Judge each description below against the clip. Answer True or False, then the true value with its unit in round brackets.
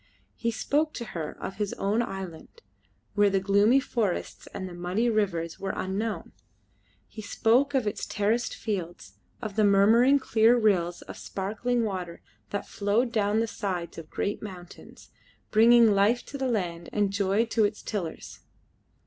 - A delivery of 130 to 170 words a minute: True (155 wpm)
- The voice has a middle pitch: False (205 Hz)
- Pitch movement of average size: True (3.2 semitones)